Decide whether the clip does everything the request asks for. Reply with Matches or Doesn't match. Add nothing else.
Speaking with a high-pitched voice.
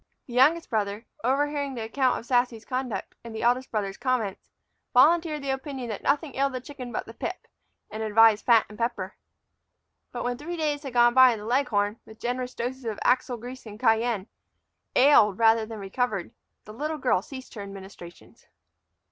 Matches